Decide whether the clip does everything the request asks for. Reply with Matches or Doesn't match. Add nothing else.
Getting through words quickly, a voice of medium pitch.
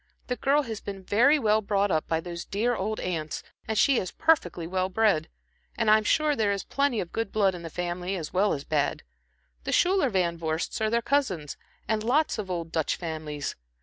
Doesn't match